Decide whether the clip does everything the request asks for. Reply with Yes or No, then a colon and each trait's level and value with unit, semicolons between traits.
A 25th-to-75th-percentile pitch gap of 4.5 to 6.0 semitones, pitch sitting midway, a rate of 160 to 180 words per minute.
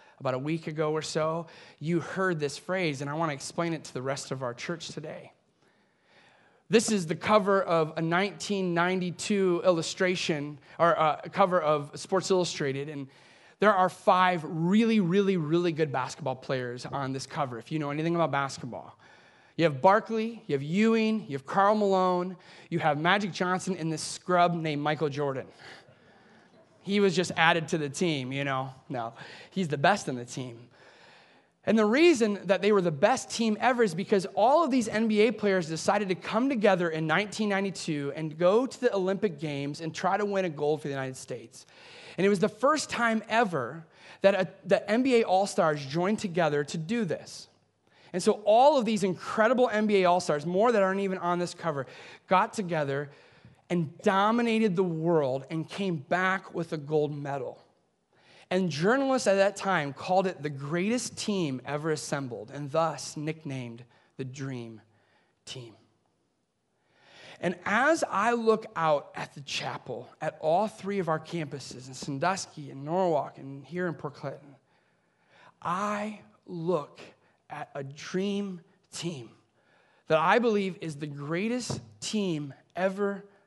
Yes: average, 5.0 semitones; medium, 175 Hz; average, 165 wpm